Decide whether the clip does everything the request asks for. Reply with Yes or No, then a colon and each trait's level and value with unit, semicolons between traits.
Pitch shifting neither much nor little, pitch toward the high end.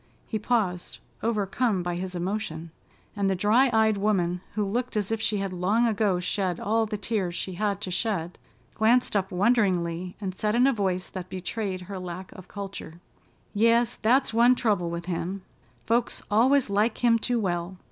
Yes: average, 3.6 semitones; high, 200 Hz